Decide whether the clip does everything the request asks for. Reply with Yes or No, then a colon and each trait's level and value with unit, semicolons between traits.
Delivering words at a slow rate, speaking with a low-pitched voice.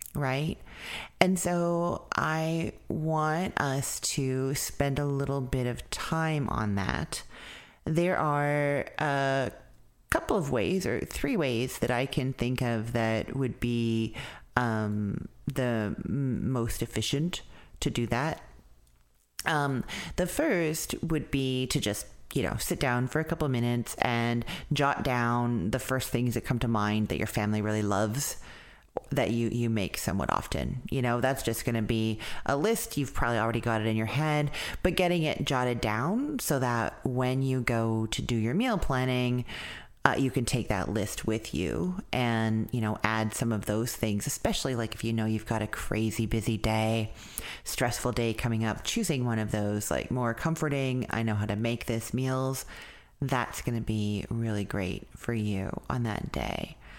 No: average, 170 wpm; low, 120 Hz